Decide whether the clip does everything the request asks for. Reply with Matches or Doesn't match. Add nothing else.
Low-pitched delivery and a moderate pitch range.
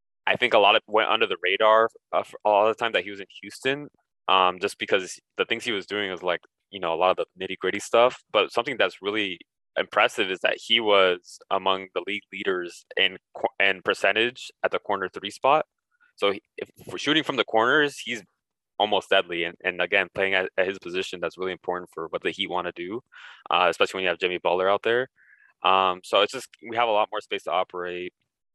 Doesn't match